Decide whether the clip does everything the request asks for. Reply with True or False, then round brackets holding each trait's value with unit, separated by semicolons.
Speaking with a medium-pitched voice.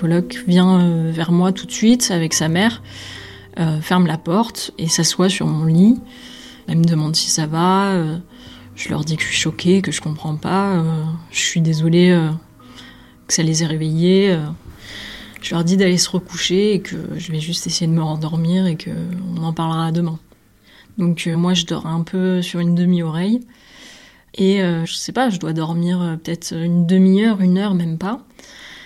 True (170 Hz)